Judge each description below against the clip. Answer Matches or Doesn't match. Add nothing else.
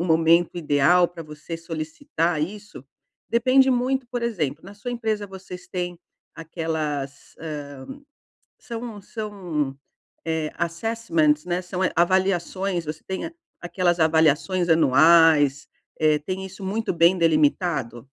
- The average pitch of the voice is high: Doesn't match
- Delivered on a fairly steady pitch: Doesn't match